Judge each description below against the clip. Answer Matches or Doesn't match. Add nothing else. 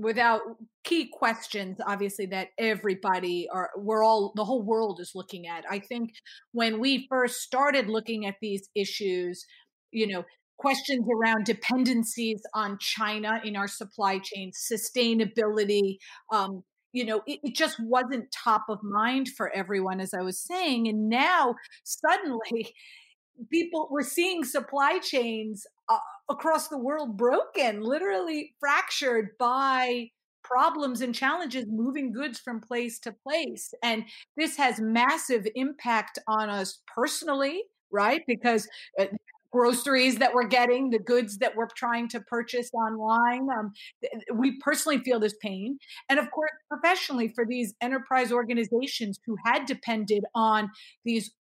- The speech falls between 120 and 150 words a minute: Matches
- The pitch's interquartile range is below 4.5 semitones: Matches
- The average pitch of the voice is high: Matches